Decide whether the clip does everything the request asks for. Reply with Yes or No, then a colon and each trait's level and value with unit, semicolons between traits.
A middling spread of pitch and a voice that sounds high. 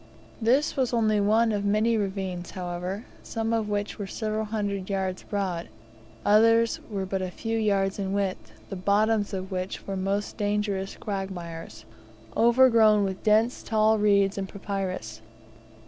No: narrow, 2.2 semitones; high, 205 Hz